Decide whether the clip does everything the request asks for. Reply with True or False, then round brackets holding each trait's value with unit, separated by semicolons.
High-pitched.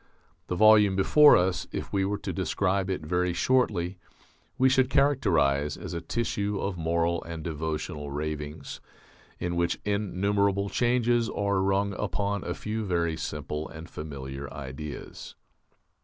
False (90 Hz)